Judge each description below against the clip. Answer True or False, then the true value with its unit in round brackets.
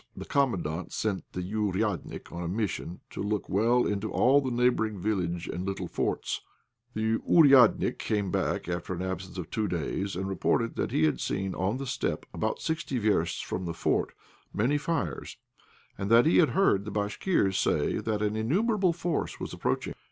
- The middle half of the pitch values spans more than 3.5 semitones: True (4.8 semitones)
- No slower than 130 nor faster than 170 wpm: False (180 wpm)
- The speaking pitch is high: False (105 Hz)